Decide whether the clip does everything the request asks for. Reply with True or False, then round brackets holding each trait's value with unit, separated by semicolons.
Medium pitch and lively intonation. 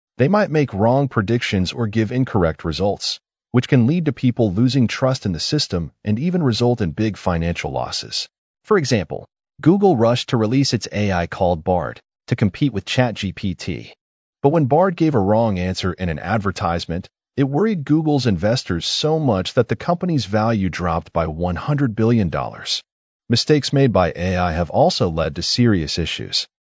False (115 Hz; 7.0 semitones)